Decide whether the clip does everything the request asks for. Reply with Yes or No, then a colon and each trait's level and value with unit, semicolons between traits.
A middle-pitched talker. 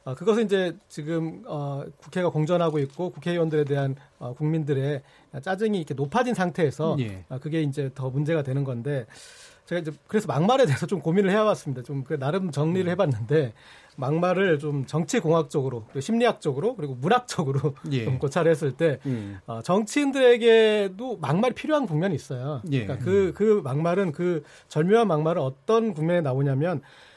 Yes: medium, 160 Hz